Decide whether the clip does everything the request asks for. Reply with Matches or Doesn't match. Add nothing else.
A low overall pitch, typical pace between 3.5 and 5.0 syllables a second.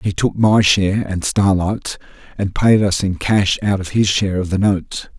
Matches